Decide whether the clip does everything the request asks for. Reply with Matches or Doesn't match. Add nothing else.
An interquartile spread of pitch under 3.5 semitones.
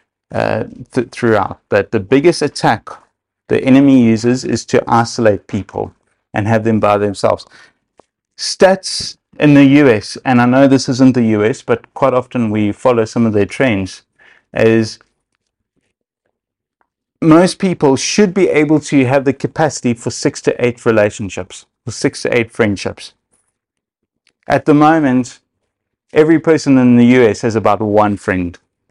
Doesn't match